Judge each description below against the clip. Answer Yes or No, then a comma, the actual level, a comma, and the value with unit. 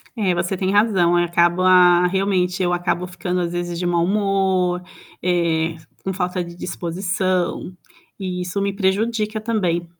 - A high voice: No, medium, 180 Hz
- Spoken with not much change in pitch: Yes, narrow, 1.7 semitones